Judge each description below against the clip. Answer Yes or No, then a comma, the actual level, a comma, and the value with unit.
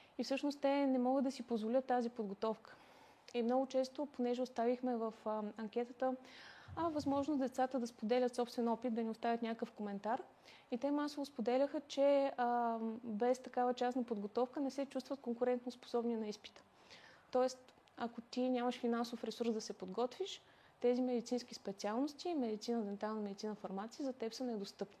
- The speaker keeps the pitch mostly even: Yes, narrow, 2.3 semitones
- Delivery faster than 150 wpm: Yes, average, 160 wpm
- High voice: Yes, high, 245 Hz